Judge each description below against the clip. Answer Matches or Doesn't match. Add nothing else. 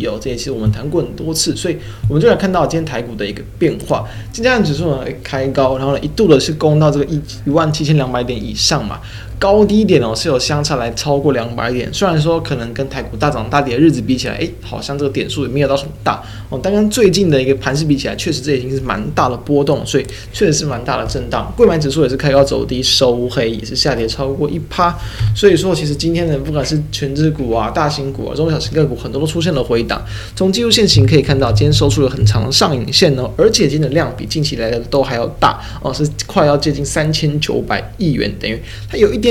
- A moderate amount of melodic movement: Matches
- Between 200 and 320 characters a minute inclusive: Doesn't match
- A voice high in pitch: Doesn't match